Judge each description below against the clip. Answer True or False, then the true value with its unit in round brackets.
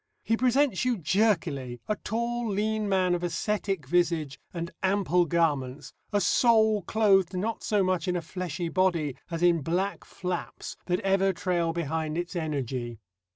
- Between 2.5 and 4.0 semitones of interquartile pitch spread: True (3.7 semitones)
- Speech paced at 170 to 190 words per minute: False (155 wpm)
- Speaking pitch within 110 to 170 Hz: False (180 Hz)